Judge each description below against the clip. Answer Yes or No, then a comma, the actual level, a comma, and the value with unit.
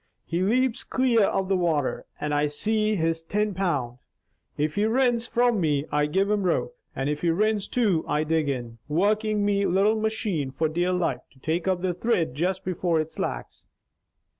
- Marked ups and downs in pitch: Yes, wide, 5.7 semitones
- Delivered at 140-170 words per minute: No, average, 185 wpm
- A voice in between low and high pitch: Yes, medium, 180 Hz